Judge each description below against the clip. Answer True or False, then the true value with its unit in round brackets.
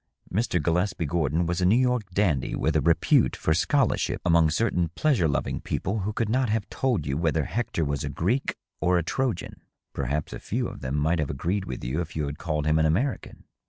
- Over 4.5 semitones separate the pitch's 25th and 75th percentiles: True (5.5 semitones)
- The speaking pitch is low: True (85 Hz)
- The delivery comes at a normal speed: False (215 wpm)